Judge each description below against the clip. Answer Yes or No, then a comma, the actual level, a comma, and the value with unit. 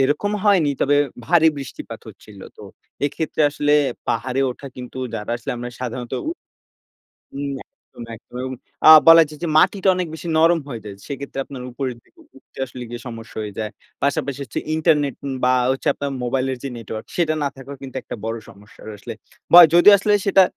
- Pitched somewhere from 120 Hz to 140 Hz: Yes, low, 135 Hz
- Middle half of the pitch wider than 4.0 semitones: Yes, average, 4.4 semitones